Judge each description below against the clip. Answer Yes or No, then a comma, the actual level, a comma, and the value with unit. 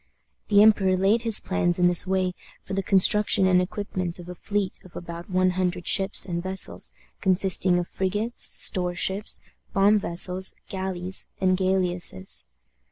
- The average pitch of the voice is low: No, medium, 185 Hz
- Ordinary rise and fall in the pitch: No, narrow, 1.4 semitones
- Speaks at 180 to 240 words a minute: No, average, 155 wpm